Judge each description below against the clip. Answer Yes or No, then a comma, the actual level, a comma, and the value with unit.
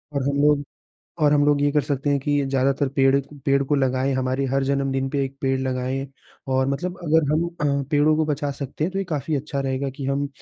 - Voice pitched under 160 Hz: Yes, medium, 140 Hz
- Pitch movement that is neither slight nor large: No, narrow, 1.7 semitones